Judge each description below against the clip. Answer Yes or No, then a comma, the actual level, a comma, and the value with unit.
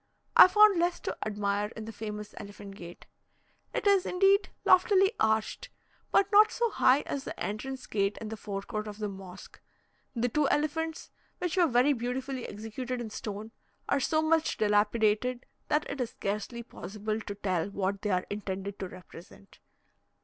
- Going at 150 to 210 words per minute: Yes, average, 170 wpm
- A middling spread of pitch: No, wide, 6.2 semitones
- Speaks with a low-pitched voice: No, high, 220 Hz